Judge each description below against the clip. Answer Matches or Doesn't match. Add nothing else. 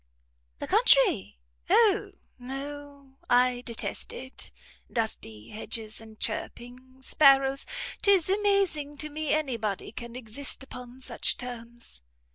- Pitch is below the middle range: Doesn't match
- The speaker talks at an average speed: Doesn't match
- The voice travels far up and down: Doesn't match